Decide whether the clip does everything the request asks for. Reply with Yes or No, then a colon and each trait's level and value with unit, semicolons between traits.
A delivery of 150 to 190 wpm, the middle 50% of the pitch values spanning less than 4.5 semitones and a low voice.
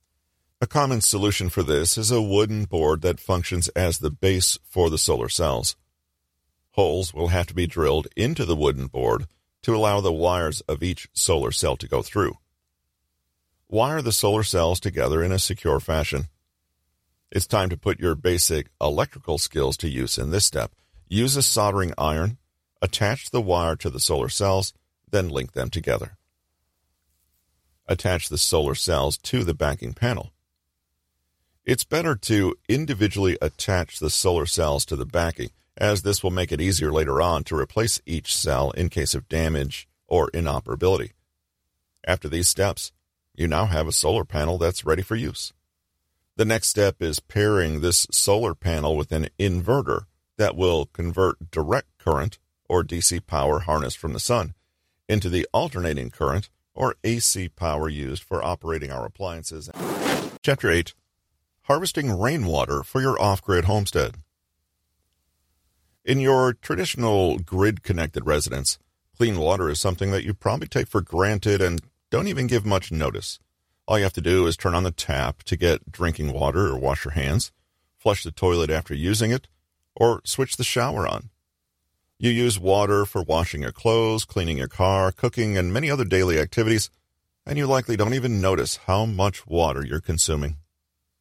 No: average, 165 wpm; average, 4.8 semitones; very low, 85 Hz